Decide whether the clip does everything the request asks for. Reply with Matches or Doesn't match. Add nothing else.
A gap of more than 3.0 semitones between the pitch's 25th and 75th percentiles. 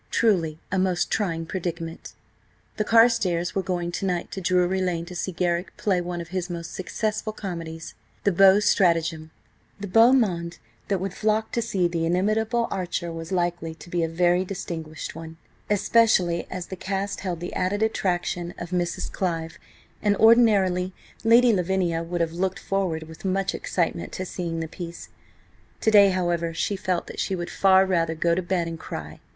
Doesn't match